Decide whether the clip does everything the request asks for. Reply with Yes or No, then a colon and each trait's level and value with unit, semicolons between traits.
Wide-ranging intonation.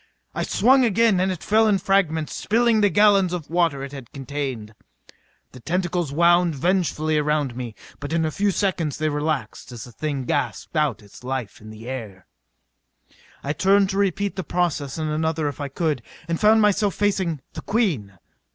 Yes: wide, 5.7 semitones